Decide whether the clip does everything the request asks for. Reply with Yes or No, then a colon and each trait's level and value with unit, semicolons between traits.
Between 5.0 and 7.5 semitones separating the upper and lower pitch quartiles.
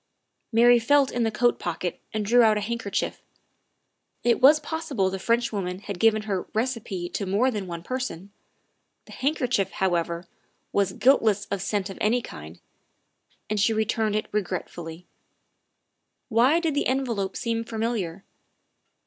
No: average, 4.0 semitones